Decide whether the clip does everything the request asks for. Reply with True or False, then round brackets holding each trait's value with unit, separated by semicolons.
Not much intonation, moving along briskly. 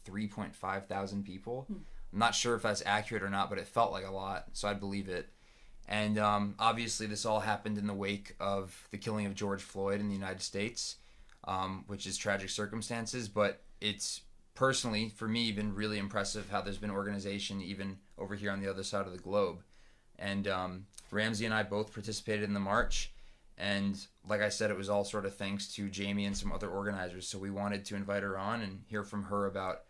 True (1.3 semitones; 210 wpm)